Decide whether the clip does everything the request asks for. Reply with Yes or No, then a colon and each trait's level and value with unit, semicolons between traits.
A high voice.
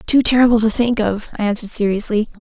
Yes: high, 220 Hz